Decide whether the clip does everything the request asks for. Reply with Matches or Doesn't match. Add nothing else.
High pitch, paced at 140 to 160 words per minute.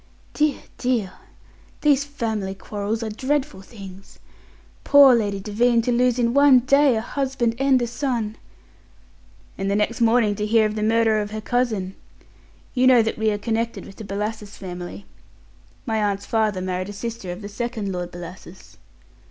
Doesn't match